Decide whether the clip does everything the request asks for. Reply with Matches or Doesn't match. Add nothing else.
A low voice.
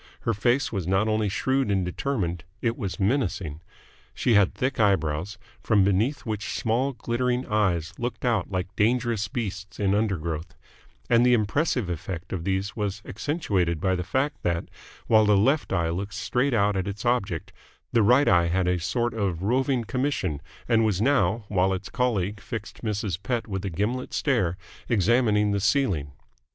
Matches